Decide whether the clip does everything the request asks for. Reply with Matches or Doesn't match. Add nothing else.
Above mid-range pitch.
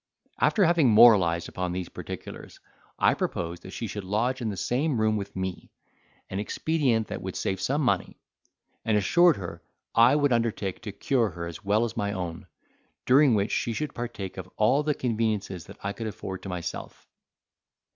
Doesn't match